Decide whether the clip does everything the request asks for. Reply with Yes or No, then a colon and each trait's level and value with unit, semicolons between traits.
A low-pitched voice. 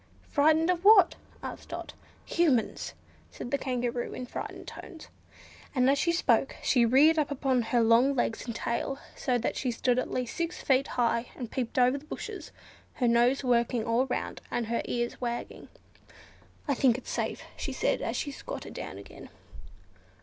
No: very high, 255 Hz